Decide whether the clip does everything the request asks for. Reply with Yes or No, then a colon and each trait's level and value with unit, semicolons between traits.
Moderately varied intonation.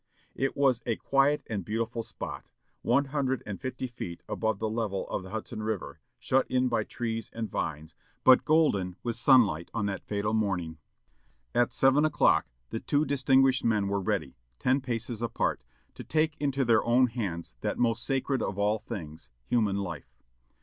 Yes: average, 4.3 semitones